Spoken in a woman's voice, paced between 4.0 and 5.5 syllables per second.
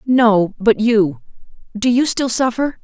No: female; 3.7 syllables/s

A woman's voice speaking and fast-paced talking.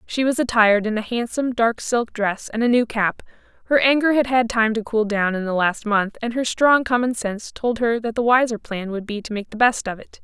Yes: female; fast, 260 wpm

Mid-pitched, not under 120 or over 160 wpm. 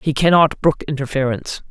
Yes: medium, 145 Hz; average, 140 wpm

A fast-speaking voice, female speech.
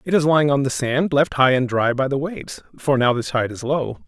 No: fast, 280 wpm; male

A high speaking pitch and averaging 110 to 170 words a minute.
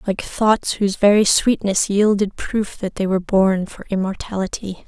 Yes: high, 200 Hz; average, 160 wpm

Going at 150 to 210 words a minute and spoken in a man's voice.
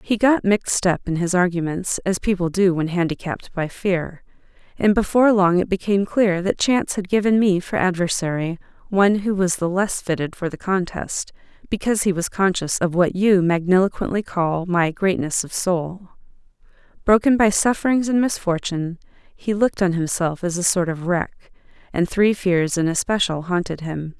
No: average, 175 wpm; female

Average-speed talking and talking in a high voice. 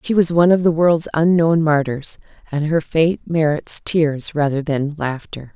No: average, 175 wpm; medium, 155 Hz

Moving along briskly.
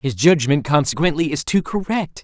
No: average, 160 wpm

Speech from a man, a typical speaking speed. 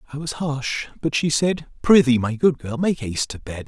No: male; fast, 230 wpm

